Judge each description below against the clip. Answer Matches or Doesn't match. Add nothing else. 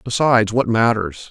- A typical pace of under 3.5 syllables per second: Doesn't match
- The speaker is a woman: Doesn't match